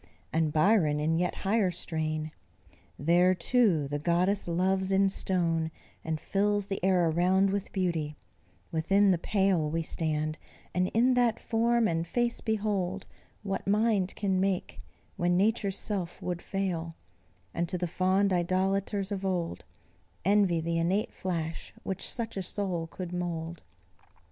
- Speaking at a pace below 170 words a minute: Yes, average, 145 wpm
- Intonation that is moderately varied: Yes, average, 3.0 semitones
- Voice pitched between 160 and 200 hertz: Yes, medium, 185 Hz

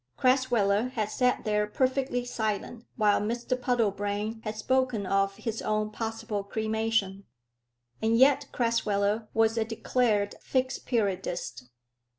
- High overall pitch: Yes, high, 220 Hz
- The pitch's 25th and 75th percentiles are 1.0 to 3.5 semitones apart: Yes, average, 3.0 semitones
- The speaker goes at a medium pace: No, slow, 120 wpm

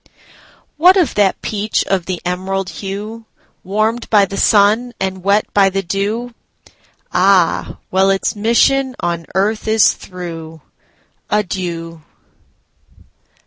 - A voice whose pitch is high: Yes, high, 195 Hz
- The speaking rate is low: Yes, slow, 105 wpm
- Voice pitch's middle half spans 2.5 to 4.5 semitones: Yes, average, 2.8 semitones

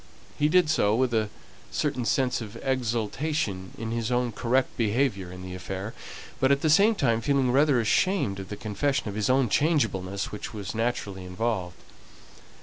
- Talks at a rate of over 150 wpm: Yes, average, 170 wpm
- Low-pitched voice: Yes, low, 115 Hz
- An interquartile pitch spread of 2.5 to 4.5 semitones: No, average, 5.0 semitones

